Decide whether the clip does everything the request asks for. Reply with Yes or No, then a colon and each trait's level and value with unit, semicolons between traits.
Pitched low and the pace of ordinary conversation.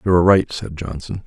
No: very low, 85 Hz; fast, 235 wpm